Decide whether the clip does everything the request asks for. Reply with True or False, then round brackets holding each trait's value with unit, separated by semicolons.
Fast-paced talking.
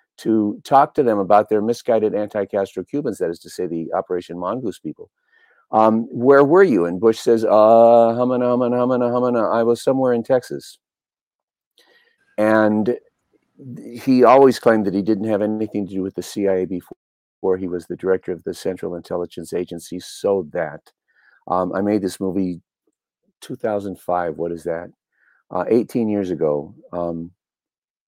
False (160 wpm)